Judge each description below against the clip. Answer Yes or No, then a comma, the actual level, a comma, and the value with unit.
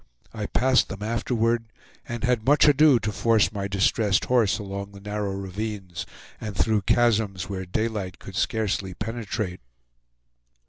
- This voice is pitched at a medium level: No, low, 105 Hz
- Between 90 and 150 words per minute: Yes, average, 140 wpm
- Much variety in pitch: No, average, 2.8 semitones